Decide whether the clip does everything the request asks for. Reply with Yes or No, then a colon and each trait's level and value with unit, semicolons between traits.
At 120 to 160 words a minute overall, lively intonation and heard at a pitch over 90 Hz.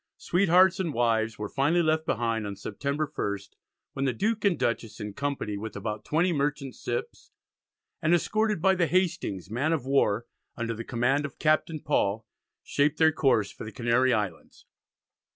No: average, 170 wpm; wide, 6.1 semitones; low, 135 Hz